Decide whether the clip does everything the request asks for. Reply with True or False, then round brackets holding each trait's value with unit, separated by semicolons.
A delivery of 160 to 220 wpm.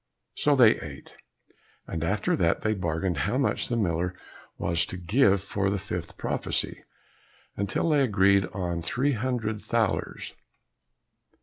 False (135 wpm)